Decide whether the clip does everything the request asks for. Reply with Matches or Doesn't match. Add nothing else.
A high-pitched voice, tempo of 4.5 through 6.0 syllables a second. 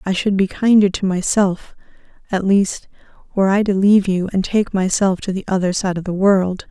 Matches